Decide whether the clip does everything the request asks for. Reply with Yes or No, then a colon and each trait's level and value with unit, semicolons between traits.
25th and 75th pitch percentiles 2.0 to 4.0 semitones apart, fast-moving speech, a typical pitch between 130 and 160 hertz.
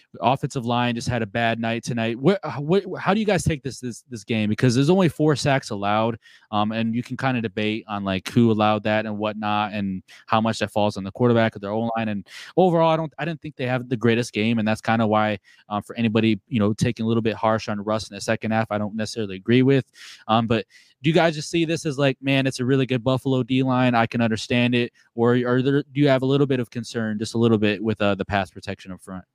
No: average, 3.5 semitones; fast, 270 wpm; low, 115 Hz